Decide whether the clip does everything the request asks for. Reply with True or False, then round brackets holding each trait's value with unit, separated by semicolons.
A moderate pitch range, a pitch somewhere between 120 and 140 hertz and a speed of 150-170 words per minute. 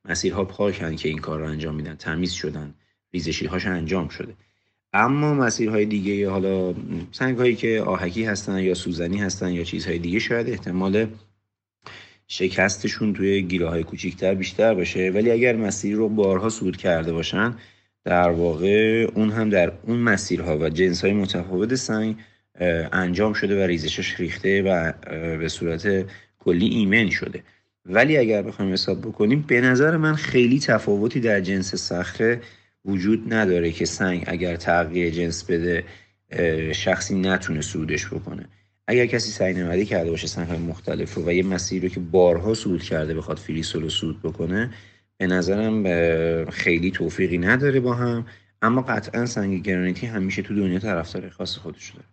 False (3.6 semitones; 95 Hz; 155 wpm)